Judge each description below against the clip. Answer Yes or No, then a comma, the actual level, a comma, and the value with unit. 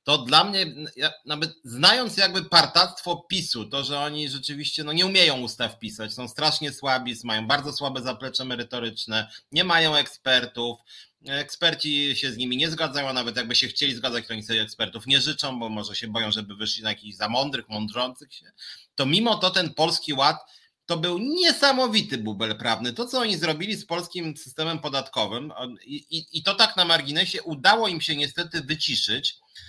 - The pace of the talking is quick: Yes, fast, 180 wpm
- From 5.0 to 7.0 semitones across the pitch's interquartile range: Yes, average, 5.3 semitones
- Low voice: No, medium, 145 Hz